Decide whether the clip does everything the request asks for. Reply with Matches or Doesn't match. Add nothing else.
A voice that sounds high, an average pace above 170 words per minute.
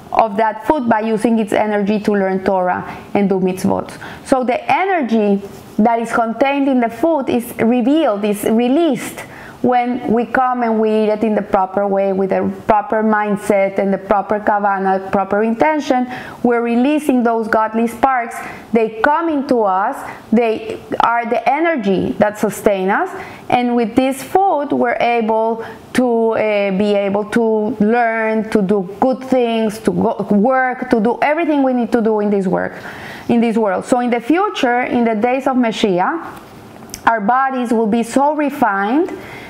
Doesn't match